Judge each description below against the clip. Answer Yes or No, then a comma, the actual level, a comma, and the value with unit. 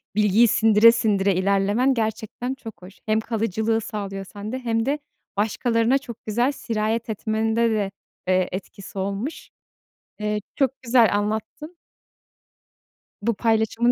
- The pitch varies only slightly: Yes, narrow, 2.3 semitones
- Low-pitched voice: No, high, 220 Hz